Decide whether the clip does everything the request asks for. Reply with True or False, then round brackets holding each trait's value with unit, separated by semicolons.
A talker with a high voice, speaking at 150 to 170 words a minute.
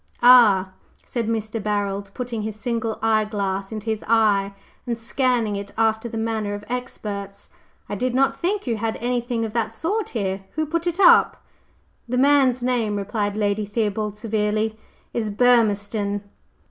True (220 Hz; 160 wpm)